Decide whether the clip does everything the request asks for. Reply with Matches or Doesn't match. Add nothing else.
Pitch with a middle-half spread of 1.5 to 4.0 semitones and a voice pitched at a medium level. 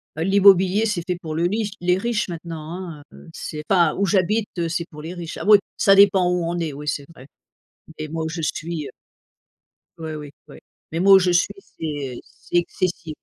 Matches